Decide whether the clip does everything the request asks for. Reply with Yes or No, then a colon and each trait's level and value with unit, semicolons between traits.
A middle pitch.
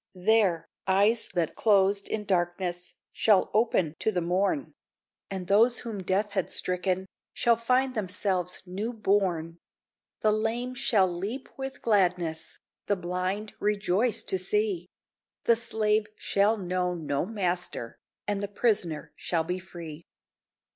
No: high, 195 Hz